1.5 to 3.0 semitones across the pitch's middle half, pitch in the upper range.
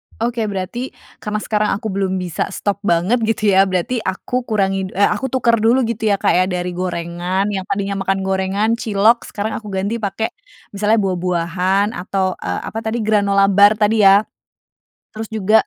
Yes: narrow, 2.6 semitones; high, 200 Hz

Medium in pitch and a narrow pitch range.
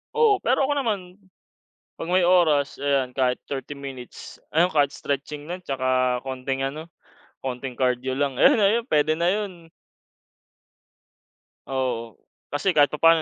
No: medium, 145 Hz; average, 5.1 semitones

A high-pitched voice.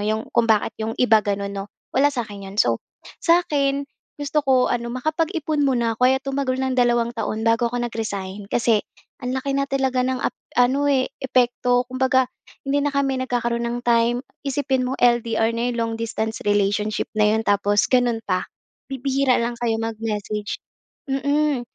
Yes: high, 240 Hz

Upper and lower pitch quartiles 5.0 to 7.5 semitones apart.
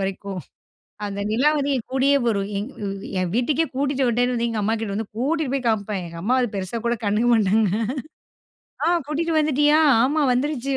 Yes: average, 5.3 semitones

